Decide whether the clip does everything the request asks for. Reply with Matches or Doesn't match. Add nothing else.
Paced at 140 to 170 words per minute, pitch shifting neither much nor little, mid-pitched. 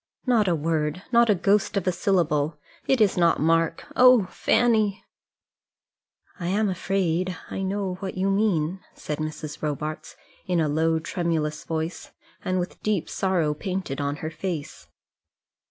Matches